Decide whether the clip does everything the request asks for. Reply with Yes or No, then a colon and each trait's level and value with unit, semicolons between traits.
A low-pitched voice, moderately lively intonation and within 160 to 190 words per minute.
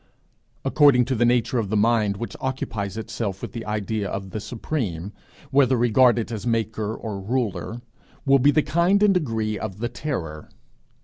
Yes: low, 115 Hz; average, 3.7 semitones; average, 170 wpm